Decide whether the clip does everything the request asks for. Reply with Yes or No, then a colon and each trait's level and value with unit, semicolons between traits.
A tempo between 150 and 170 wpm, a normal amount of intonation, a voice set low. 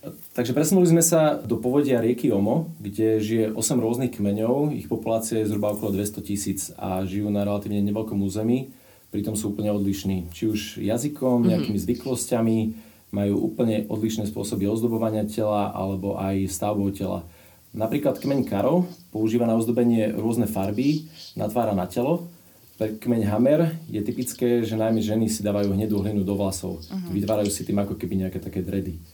Yes: average, 160 wpm; average, 3.0 semitones; low, 110 Hz